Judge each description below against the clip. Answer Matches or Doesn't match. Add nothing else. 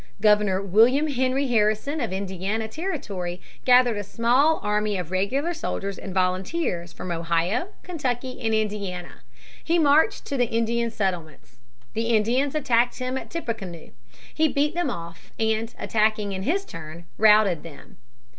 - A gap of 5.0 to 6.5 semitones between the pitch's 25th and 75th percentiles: Matches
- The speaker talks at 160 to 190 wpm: Doesn't match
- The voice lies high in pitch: Matches